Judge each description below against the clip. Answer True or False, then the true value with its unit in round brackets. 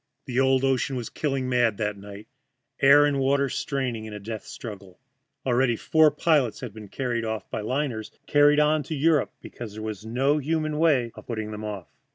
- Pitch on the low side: True (125 Hz)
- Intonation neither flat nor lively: True (4.6 semitones)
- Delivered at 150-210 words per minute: True (200 wpm)